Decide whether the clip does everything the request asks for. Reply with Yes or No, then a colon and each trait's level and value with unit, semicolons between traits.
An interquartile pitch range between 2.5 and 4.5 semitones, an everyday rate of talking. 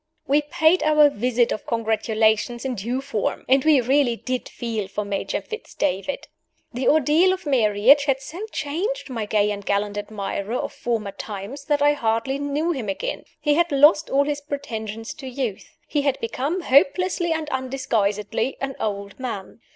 No: average, 5.1 semitones; average, 170 wpm